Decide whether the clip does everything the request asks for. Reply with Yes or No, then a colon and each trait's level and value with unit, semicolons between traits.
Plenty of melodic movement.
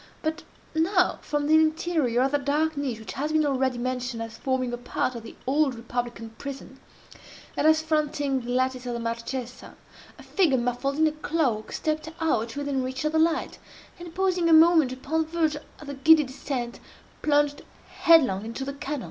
No: average, 3.8 semitones